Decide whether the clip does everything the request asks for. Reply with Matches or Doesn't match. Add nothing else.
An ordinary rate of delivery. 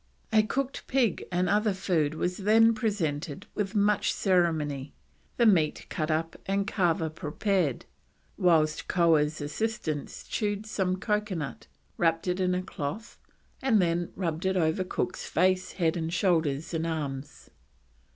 Doesn't match